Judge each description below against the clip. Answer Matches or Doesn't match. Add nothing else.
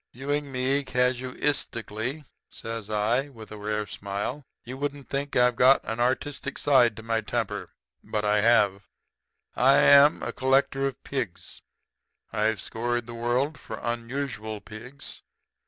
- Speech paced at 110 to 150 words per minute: Matches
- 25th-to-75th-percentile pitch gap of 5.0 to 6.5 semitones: Doesn't match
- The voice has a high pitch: Doesn't match